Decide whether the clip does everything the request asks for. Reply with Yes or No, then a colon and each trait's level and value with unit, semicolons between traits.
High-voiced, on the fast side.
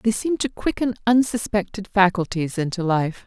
No: high, 205 Hz; average, 145 wpm